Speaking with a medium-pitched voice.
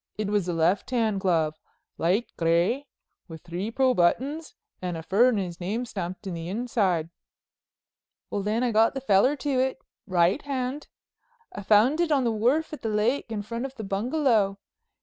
No: high, 215 Hz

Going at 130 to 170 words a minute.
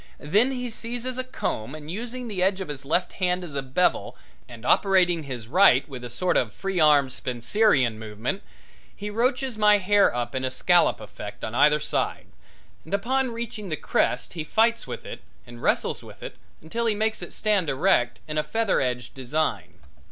No: average, 190 wpm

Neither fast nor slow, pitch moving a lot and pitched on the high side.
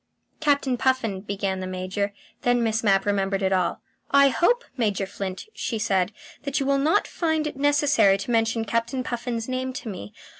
Yes: average, 180 wpm; wide, 5.7 semitones; high, 230 Hz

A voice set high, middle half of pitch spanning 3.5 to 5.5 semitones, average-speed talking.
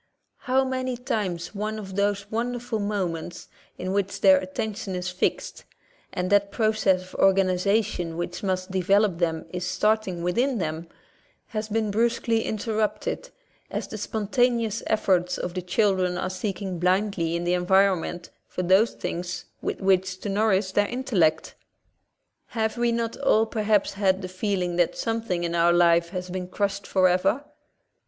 No: high, 195 Hz; average, 3.1 semitones; average, 155 wpm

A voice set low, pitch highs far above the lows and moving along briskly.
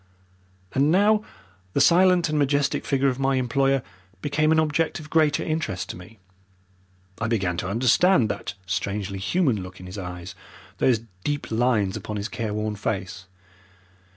No: low, 125 Hz; wide, 7.1 semitones; average, 155 wpm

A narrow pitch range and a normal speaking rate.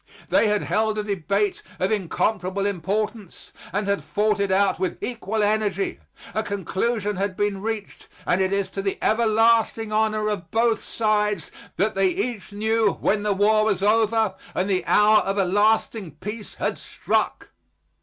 Yes: narrow, 1.8 semitones; average, 165 wpm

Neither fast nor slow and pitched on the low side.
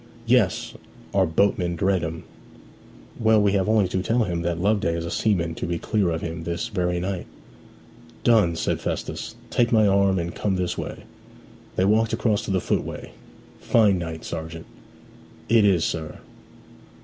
Yes: average, 165 wpm; very low, 95 Hz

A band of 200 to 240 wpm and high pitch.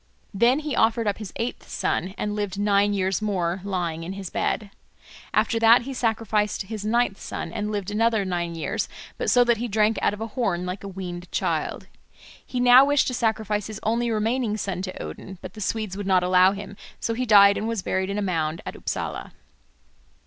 Yes: fast, 205 wpm; high, 205 Hz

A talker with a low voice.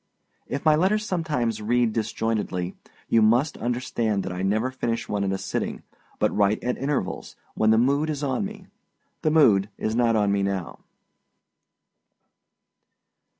Yes: low, 115 Hz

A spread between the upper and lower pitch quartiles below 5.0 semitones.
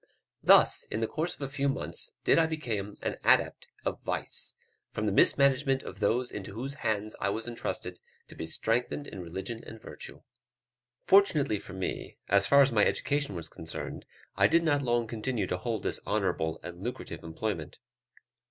No: wide, 5.6 semitones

